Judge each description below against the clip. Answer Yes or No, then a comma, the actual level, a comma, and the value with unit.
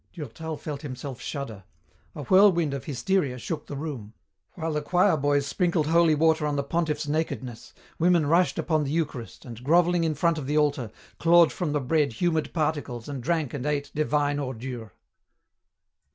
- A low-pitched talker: No, medium, 150 Hz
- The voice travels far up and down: No, average, 2.9 semitones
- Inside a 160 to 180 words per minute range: Yes, average, 170 wpm